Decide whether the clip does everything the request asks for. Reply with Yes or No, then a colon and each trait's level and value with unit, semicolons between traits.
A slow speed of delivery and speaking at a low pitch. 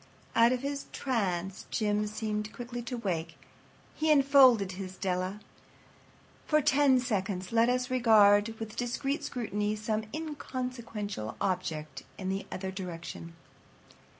No: slow, 125 wpm; high, 215 Hz